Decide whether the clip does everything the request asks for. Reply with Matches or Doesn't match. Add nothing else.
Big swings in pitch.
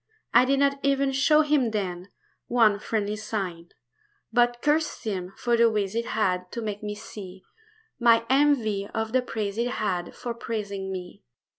Doesn't match